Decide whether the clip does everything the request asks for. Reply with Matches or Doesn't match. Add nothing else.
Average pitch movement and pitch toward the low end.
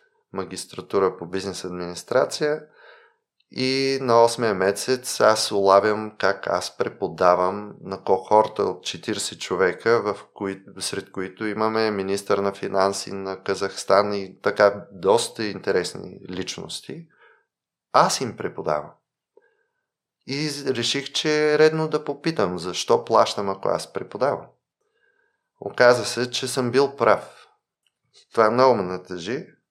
Doesn't match